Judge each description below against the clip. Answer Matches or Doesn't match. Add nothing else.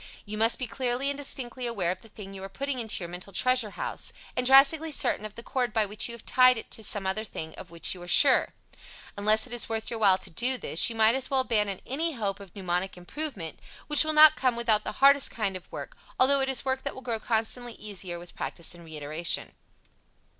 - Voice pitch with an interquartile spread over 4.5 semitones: Matches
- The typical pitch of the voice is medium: Doesn't match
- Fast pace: Matches